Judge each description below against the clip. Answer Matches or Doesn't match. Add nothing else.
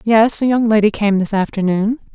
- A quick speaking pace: Doesn't match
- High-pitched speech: Matches